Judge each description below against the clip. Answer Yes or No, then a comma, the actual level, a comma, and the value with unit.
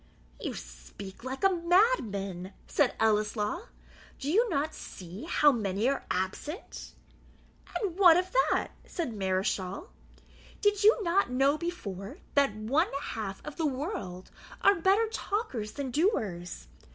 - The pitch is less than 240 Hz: No, very high, 275 Hz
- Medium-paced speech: No, slow, 130 wpm